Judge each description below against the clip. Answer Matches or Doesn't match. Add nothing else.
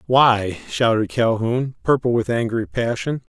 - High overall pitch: Doesn't match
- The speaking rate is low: Matches